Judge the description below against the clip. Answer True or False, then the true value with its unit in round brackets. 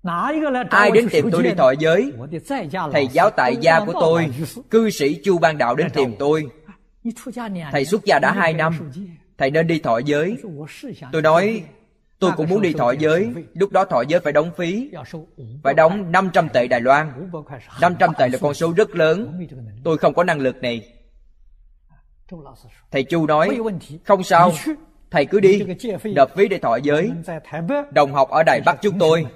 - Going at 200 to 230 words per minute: False (175 wpm)